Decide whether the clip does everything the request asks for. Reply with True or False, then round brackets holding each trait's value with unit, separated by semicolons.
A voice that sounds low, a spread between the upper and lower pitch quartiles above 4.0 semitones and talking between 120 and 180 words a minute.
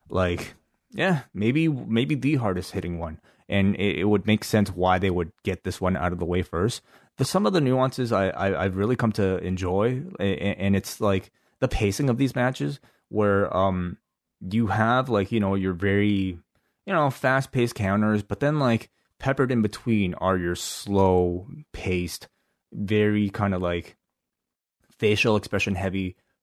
True (100 Hz; 4.5 semitones; 175 wpm)